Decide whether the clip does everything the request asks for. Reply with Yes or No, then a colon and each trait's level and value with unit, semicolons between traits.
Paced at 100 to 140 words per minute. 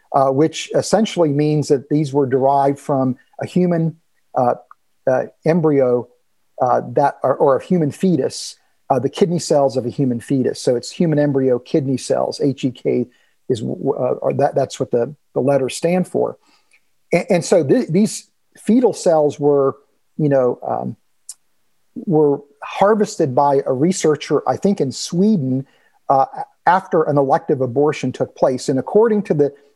No: average, 160 wpm